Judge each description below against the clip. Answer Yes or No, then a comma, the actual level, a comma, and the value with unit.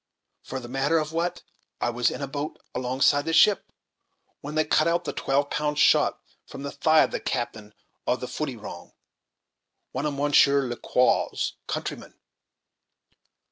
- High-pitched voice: No, medium, 145 Hz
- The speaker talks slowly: No, average, 160 wpm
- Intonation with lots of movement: No, average, 2.7 semitones